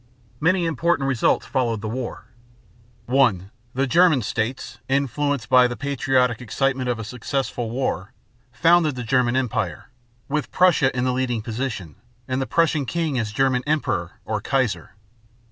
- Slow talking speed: No, average, 145 wpm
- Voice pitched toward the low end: Yes, low, 130 Hz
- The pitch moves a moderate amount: Yes, average, 3.1 semitones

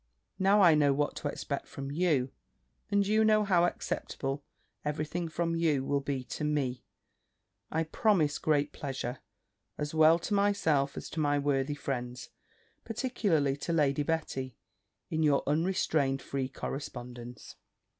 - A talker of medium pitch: Yes, medium, 150 Hz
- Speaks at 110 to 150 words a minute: Yes, average, 145 wpm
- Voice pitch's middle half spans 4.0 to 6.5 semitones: No, average, 3.5 semitones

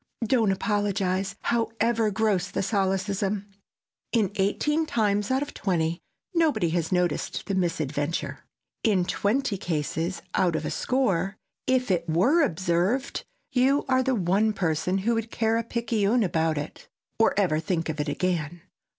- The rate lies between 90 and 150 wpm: Yes, average, 145 wpm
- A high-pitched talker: Yes, high, 195 Hz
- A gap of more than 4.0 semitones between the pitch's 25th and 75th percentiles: Yes, average, 4.7 semitones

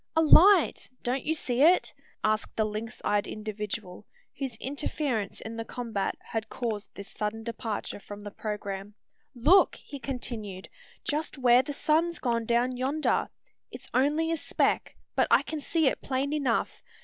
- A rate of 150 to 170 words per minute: Yes, average, 160 wpm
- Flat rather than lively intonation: No, average, 5.2 semitones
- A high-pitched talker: Yes, high, 240 Hz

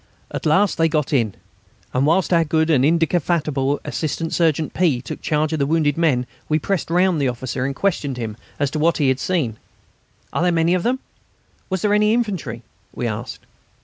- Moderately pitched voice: Yes, medium, 155 Hz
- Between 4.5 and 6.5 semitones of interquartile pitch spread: No, average, 4.1 semitones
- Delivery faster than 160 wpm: Yes, average, 195 wpm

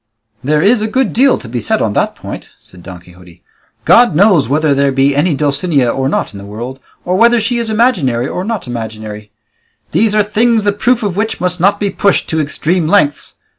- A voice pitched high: No, medium, 165 Hz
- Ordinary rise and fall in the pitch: No, wide, 8.3 semitones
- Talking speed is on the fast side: Yes, fast, 210 wpm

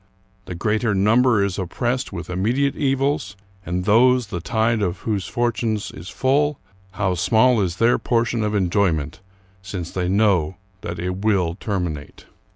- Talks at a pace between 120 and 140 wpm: No, average, 155 wpm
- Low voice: Yes, low, 105 Hz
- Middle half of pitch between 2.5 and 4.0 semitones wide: No, average, 4.5 semitones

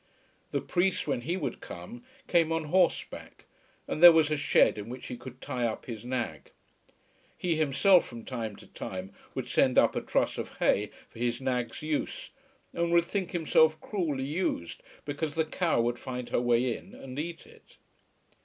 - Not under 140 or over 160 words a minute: No, average, 180 wpm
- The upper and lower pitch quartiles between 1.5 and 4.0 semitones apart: No, wide, 5.6 semitones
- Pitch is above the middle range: No, medium, 145 Hz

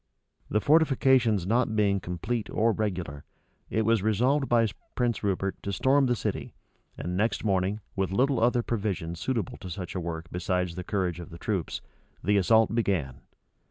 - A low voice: Yes, low, 105 Hz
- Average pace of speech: Yes, average, 165 wpm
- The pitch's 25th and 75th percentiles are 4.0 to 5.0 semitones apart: Yes, average, 4.3 semitones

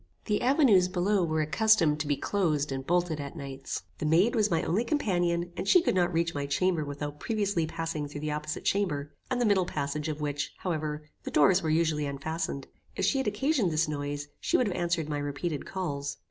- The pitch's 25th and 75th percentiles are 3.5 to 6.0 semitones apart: Yes, average, 4.4 semitones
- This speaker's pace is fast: Yes, fast, 210 wpm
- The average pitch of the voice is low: No, medium, 165 Hz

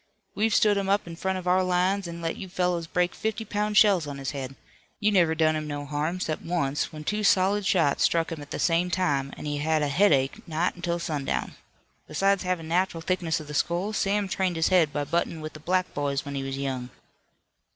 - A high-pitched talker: No, medium, 170 Hz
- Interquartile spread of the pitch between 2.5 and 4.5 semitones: Yes, average, 3.9 semitones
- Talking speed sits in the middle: No, fast, 225 wpm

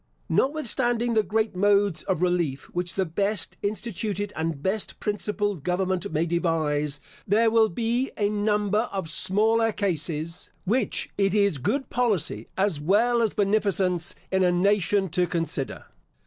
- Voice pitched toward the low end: No, high, 200 Hz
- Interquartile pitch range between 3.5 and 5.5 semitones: Yes, average, 3.8 semitones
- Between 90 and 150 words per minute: Yes, average, 140 wpm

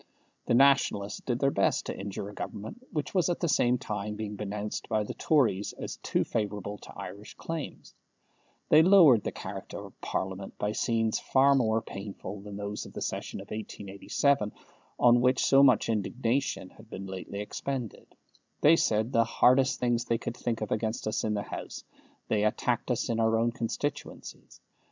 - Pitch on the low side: Yes, low, 115 Hz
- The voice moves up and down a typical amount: Yes, average, 3.9 semitones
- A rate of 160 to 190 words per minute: Yes, average, 175 wpm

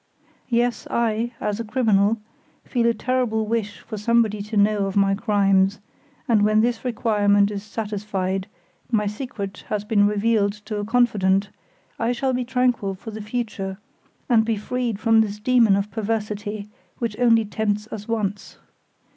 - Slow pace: No, average, 155 wpm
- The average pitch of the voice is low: No, high, 215 Hz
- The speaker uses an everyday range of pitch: No, narrow, 2.3 semitones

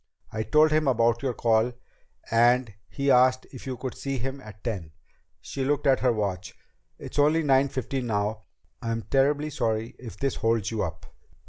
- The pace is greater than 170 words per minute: Yes, average, 180 wpm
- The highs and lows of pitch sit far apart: No, average, 3.4 semitones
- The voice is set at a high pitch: No, low, 125 Hz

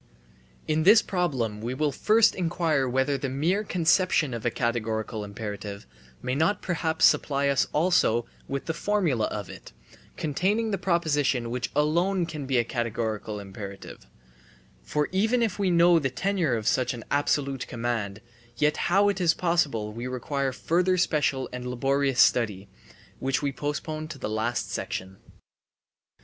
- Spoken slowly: No, average, 155 wpm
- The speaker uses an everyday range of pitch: No, wide, 6.3 semitones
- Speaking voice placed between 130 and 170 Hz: Yes, medium, 140 Hz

